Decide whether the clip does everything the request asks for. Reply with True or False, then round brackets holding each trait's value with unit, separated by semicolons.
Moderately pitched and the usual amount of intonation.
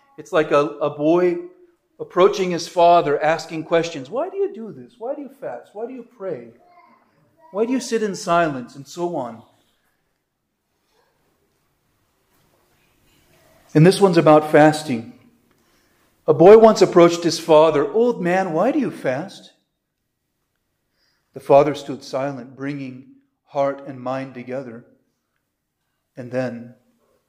False (165 Hz; 7.4 semitones)